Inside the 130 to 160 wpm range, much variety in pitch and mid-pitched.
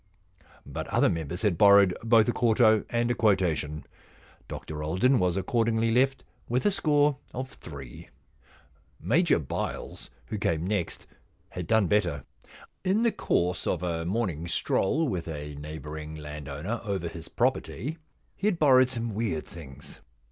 No: average, 150 wpm; wide, 6.9 semitones; low, 100 Hz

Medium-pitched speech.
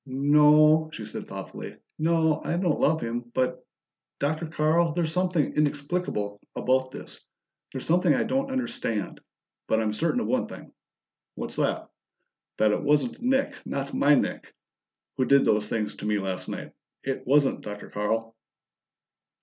Yes: medium, 145 Hz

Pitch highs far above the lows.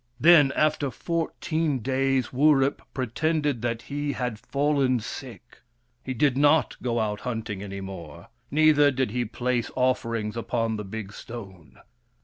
No: average, 4.3 semitones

